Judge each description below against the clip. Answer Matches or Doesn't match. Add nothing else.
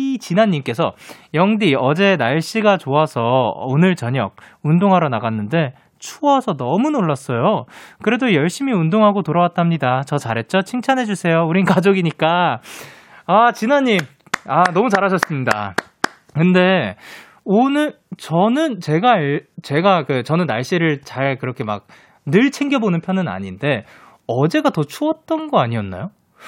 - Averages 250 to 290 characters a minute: Matches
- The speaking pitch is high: Doesn't match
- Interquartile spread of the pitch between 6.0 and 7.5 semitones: Matches